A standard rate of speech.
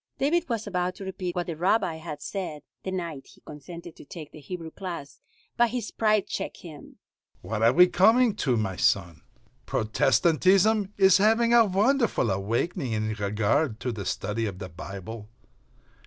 Yes: average, 170 wpm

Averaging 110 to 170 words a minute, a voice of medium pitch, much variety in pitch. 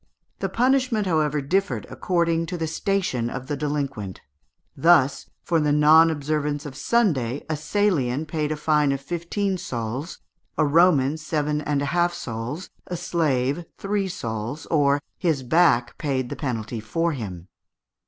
No: average, 150 wpm; medium, 150 Hz; average, 4.2 semitones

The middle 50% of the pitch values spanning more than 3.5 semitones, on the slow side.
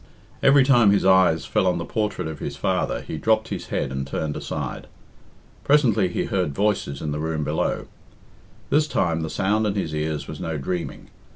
No: wide, 5.4 semitones; average, 190 wpm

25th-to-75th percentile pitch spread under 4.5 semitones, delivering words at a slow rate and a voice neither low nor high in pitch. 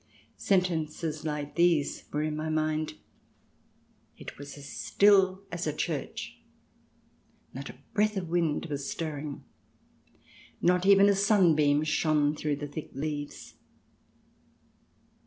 Yes: average, 3.2 semitones; slow, 125 wpm; medium, 155 Hz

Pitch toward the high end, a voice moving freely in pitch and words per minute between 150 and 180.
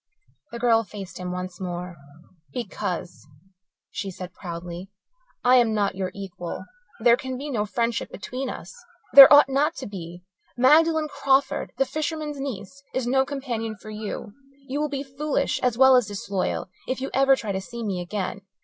Yes: high, 235 Hz; wide, 5.9 semitones; average, 170 wpm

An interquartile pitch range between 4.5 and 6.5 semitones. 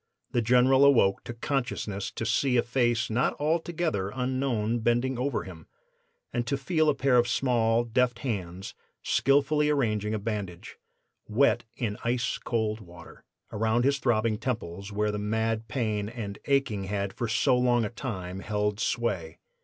No: average, 3.6 semitones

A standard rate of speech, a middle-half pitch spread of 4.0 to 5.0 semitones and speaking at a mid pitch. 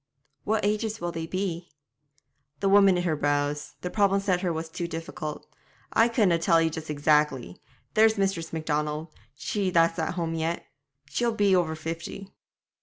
No: average, 165 wpm; average, 3.6 semitones; medium, 170 Hz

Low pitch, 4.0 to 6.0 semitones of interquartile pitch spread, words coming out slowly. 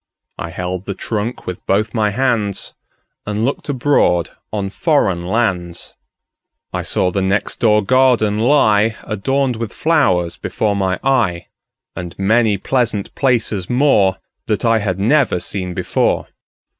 Yes: low, 105 Hz; average, 4.4 semitones; slow, 120 wpm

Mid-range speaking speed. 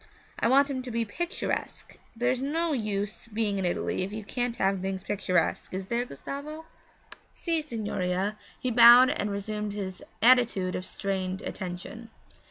Yes: average, 155 wpm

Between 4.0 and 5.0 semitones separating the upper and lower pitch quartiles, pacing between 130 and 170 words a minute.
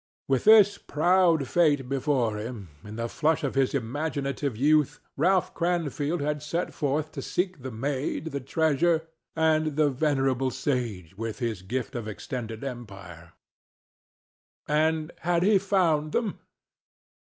Yes: average, 4.4 semitones; slow, 135 wpm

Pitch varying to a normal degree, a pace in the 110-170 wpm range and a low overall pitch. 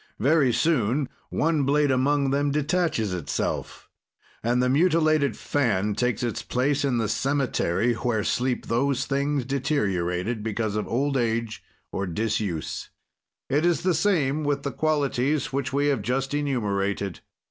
Yes: average, 4.4 semitones; average, 140 wpm; low, 130 Hz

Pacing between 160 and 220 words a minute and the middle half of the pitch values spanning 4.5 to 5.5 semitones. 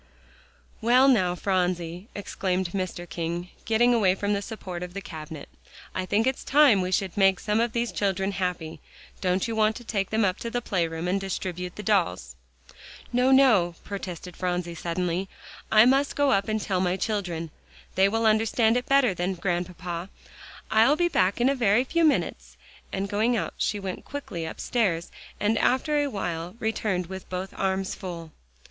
No: average, 180 wpm; average, 3.9 semitones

